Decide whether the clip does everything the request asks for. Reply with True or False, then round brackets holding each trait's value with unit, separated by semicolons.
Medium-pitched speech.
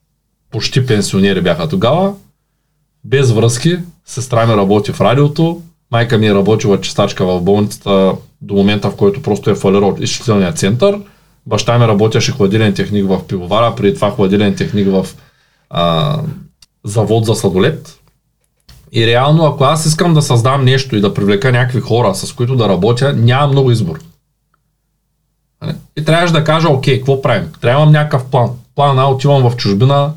False (130 Hz)